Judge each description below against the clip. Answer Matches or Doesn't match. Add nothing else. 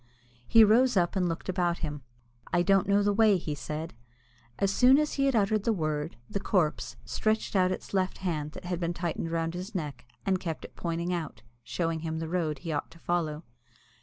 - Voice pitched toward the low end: Doesn't match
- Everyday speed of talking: Doesn't match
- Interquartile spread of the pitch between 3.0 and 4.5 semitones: Matches